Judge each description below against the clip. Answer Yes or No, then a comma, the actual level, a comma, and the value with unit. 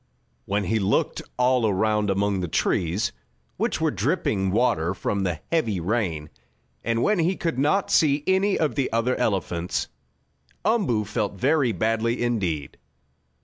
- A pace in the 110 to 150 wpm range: Yes, average, 145 wpm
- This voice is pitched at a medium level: No, low, 110 Hz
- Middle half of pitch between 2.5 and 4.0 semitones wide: No, average, 5.1 semitones